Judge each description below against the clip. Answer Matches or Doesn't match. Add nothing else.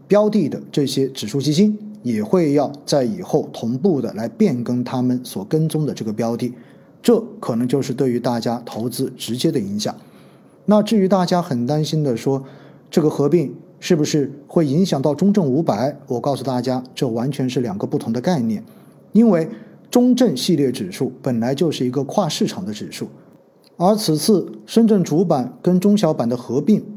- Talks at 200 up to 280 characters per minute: Matches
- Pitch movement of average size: Doesn't match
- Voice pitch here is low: Doesn't match